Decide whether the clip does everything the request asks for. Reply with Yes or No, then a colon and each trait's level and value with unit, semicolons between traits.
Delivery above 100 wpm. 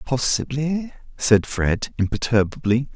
No: slow, 80 wpm